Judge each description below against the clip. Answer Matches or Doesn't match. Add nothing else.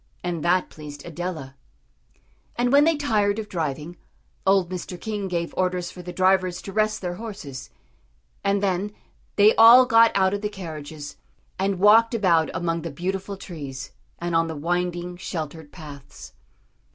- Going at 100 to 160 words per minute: Matches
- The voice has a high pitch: Doesn't match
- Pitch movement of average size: Matches